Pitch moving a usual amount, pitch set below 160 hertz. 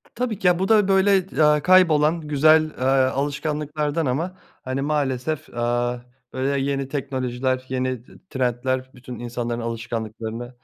Yes: average, 3.7 semitones; low, 135 Hz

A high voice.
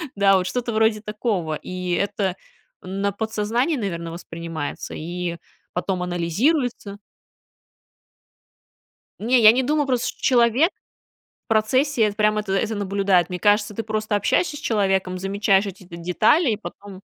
Yes: high, 205 Hz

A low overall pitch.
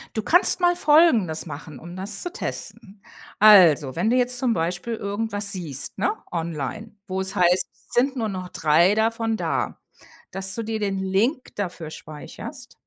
No: high, 200 Hz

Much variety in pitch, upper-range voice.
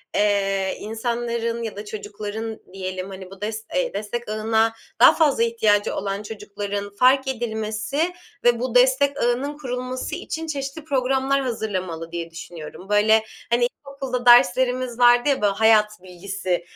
No: average, 3.7 semitones; high, 225 Hz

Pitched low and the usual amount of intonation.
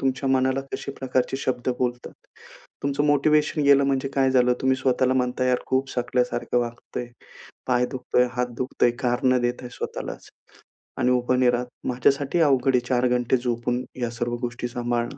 No: low, 125 Hz; narrow, 1.4 semitones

